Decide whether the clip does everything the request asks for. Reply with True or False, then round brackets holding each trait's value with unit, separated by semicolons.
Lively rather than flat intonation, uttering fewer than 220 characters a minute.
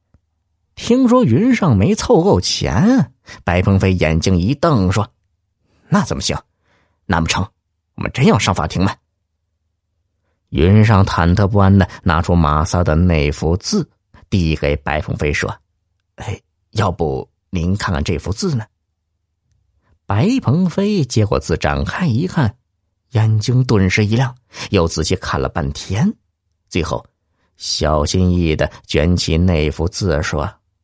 False (4.1 semitones; 190 characters per minute)